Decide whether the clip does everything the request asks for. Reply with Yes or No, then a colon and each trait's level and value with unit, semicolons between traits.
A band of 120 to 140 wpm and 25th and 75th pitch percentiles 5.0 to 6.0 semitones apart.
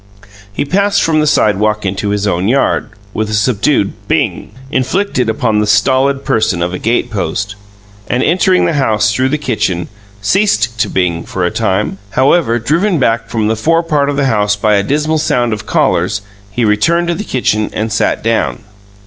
No: average, 185 wpm; average, 5.3 semitones